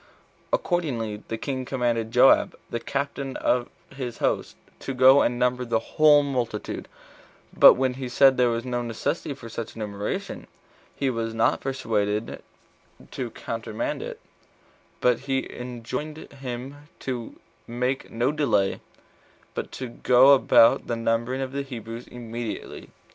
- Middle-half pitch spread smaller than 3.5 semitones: Yes, narrow, 2.6 semitones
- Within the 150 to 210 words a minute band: No, average, 140 wpm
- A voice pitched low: Yes, low, 125 Hz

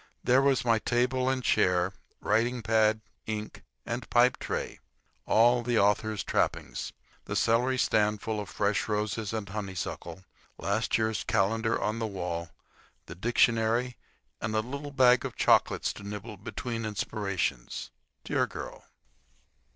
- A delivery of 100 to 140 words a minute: Yes, slow, 135 wpm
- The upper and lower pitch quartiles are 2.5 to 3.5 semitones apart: Yes, average, 2.8 semitones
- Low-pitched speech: Yes, low, 110 Hz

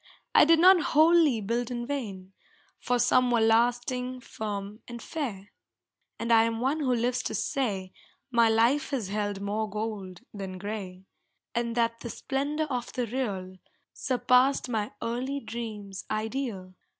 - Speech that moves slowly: No, average, 150 wpm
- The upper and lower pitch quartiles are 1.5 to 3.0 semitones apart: No, average, 3.6 semitones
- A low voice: No, high, 235 Hz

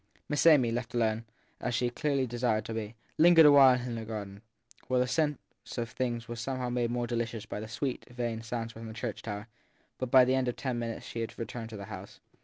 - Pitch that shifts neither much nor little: No, narrow, 2.1 semitones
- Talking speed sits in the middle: No, fast, 230 wpm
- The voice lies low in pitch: Yes, low, 120 Hz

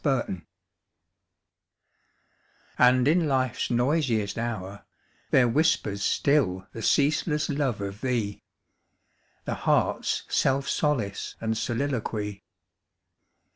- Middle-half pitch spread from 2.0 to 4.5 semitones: No, average, 5.3 semitones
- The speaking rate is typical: No, slow, 95 wpm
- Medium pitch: No, low, 125 Hz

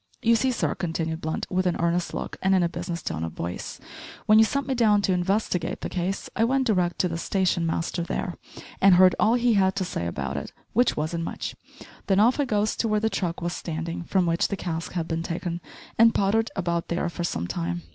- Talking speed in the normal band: No, fast, 230 wpm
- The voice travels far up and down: No, average, 3.8 semitones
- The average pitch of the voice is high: No, medium, 180 Hz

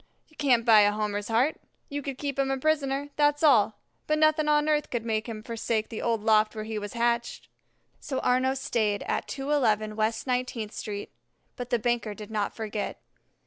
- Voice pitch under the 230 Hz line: No, high, 235 Hz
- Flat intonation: No, average, 4.3 semitones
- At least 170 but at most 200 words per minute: Yes, average, 190 wpm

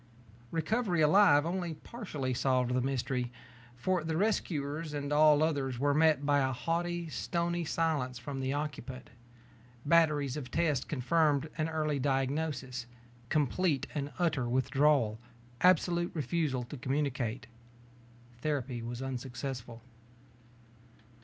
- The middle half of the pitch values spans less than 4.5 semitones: Yes, average, 3.7 semitones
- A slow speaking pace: Yes, slow, 115 wpm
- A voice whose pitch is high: No, medium, 145 Hz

